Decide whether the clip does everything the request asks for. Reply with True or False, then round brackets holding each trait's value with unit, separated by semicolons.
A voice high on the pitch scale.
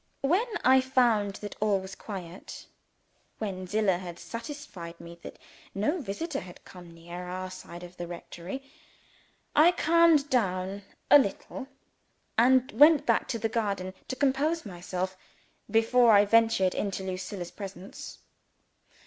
True (205 Hz)